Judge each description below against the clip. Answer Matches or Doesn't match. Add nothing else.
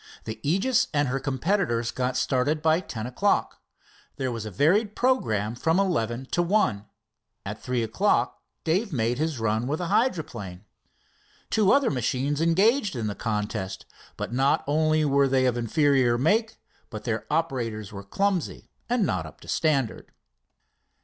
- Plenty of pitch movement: Matches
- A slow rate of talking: Doesn't match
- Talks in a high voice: Doesn't match